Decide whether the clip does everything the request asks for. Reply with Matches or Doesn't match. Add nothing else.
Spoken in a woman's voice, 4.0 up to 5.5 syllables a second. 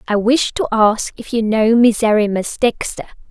Matches